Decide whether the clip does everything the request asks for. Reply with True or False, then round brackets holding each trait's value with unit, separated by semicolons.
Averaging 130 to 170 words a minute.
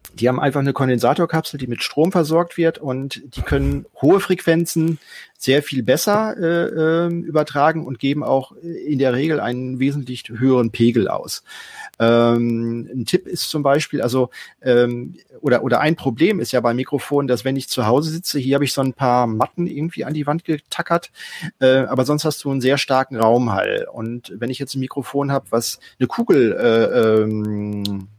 False (185 wpm)